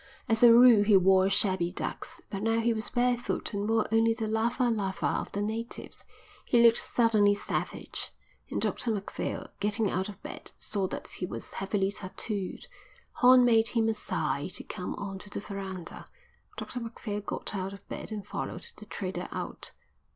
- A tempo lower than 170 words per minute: No, average, 180 wpm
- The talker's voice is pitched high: Yes, high, 210 Hz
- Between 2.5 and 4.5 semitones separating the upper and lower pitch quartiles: Yes, average, 2.8 semitones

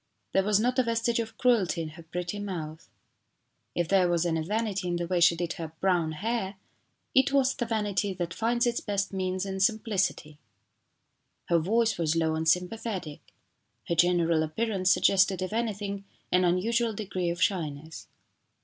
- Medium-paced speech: Yes, average, 165 wpm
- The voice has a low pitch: No, high, 190 Hz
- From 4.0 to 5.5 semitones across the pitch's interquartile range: Yes, average, 4.4 semitones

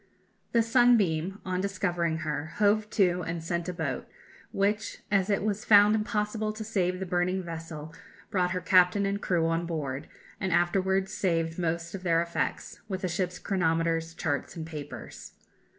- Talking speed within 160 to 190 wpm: Yes, average, 165 wpm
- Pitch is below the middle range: No, medium, 180 Hz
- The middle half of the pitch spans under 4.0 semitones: Yes, average, 3.3 semitones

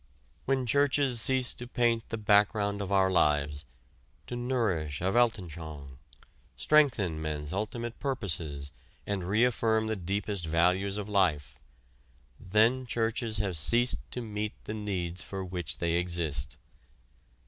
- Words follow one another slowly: Yes, slow, 125 wpm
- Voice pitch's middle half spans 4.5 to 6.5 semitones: Yes, wide, 5.4 semitones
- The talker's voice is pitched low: Yes, low, 100 Hz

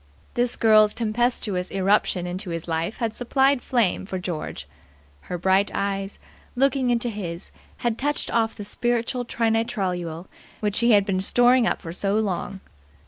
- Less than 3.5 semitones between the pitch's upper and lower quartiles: No, average, 4.2 semitones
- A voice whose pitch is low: No, high, 210 Hz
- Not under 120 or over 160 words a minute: Yes, average, 150 wpm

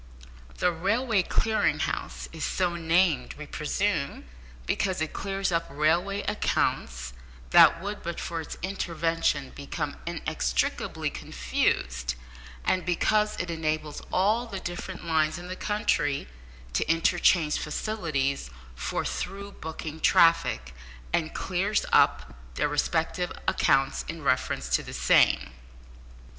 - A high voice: No, medium, 165 Hz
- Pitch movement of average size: Yes, average, 4.0 semitones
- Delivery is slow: Yes, slow, 120 wpm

